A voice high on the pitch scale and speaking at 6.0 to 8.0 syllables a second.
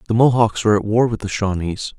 No: low, 110 Hz; 6.2 syllables/s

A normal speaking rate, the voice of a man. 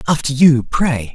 Yes: average, 160 wpm; male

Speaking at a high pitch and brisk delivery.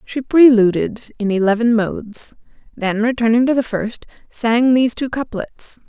No: high, 230 Hz; average, 145 wpm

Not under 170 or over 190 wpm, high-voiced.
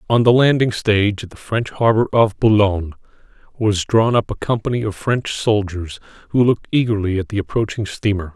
No: average, 180 wpm; low, 105 Hz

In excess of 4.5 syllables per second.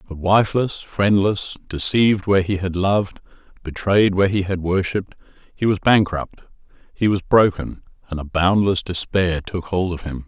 Yes: 5.1 syllables/s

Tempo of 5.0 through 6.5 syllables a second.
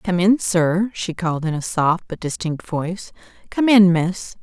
No: 4.3 syllables/s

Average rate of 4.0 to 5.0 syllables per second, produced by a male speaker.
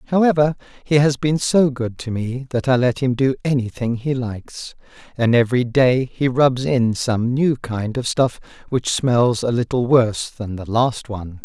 Yes: 4.5 syllables/s; male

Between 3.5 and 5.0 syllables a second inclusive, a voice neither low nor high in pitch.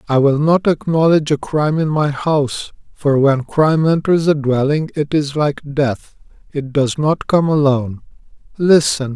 Yes: 4.6 syllables/s; medium, 145 Hz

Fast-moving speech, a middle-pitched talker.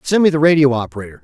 Yes: fast, 240 wpm; medium, 145 Hz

